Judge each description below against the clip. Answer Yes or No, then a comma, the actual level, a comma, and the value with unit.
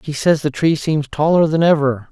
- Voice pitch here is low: No, medium, 150 Hz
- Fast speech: Yes, fast, 225 wpm